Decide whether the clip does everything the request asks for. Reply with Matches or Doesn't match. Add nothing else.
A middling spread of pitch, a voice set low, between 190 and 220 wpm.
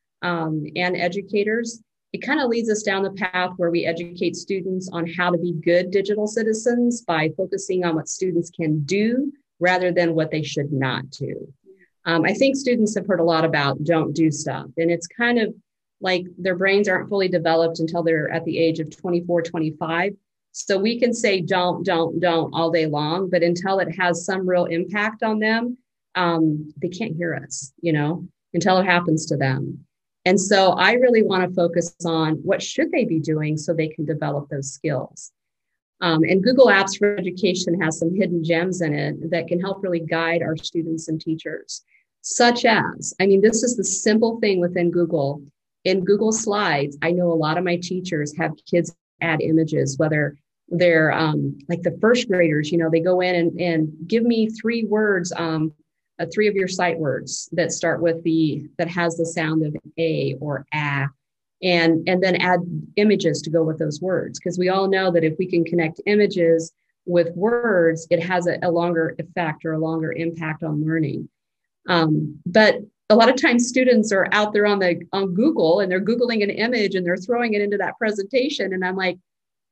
Doesn't match